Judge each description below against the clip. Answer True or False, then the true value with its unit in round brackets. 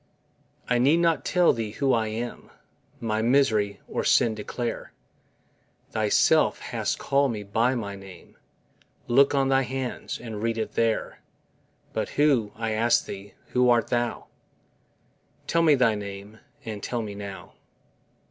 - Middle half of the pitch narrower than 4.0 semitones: True (3.4 semitones)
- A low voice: True (115 Hz)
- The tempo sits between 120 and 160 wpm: True (145 wpm)